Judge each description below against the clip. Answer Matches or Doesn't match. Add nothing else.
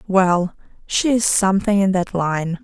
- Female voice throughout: Matches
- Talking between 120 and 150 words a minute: Matches